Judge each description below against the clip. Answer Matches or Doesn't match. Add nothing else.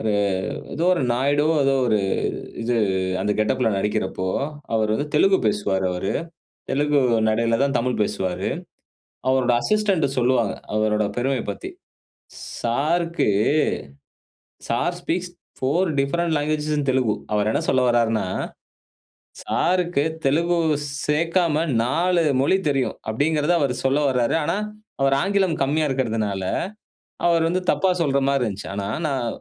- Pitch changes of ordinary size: Doesn't match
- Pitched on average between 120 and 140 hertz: Matches